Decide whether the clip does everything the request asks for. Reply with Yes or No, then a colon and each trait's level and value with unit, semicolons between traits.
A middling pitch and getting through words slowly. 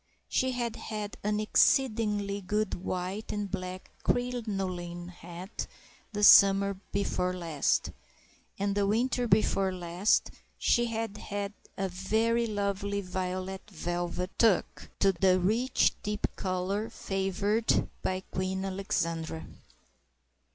No: high, 195 Hz; slow, 105 wpm